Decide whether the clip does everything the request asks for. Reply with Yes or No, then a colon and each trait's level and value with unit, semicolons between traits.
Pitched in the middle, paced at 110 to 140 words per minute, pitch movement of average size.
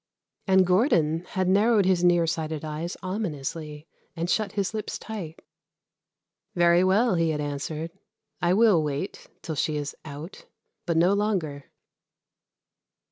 Yes: medium, 170 Hz; slow, 135 wpm; average, 3.5 semitones